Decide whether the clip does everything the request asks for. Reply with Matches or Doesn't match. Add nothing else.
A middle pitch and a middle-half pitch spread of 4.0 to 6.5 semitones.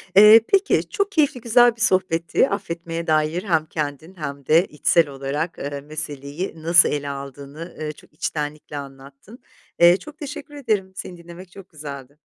Matches